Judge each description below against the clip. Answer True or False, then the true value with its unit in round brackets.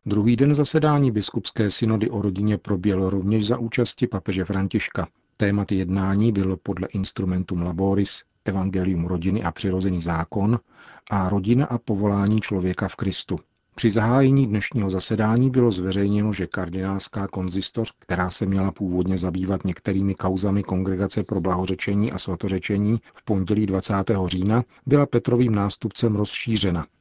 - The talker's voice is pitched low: True (100 Hz)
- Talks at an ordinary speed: True (135 wpm)